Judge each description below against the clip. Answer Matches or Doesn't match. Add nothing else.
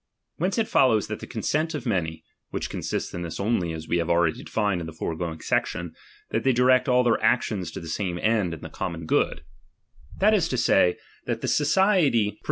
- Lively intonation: Matches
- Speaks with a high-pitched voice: Doesn't match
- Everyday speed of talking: Doesn't match